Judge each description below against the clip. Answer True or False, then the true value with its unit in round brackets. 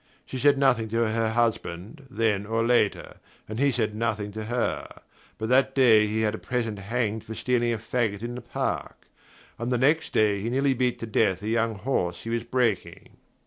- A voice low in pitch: True (115 Hz)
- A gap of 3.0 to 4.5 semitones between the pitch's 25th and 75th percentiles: False (2.4 semitones)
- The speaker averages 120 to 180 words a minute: False (200 wpm)